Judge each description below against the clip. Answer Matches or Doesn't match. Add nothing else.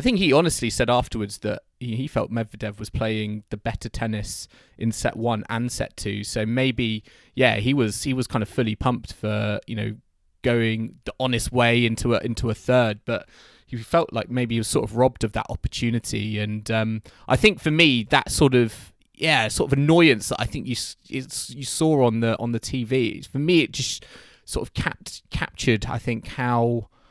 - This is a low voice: Matches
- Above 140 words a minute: Matches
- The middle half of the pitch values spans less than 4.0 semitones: Matches